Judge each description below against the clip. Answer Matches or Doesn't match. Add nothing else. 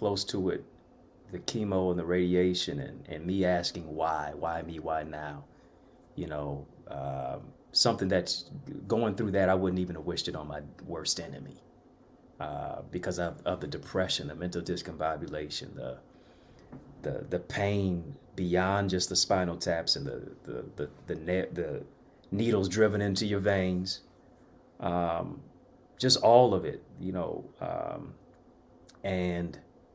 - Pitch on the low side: Matches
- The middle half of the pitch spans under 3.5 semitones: Matches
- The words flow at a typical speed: Matches